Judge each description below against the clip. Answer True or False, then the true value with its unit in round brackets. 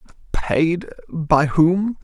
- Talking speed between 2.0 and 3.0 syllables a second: True (2.6 syllables/s)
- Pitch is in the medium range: True (165 Hz)